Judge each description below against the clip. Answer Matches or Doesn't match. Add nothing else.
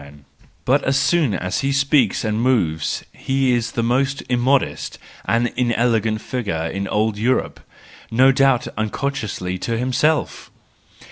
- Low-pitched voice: Matches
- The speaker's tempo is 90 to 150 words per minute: Matches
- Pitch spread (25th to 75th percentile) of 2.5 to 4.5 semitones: Matches